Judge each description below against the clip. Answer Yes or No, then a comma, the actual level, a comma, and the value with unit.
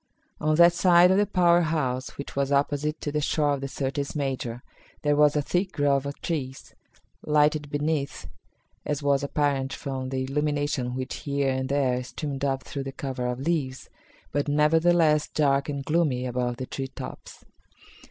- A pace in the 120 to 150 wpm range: No, average, 170 wpm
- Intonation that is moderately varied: No, narrow, 2.3 semitones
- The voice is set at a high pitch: No, medium, 140 Hz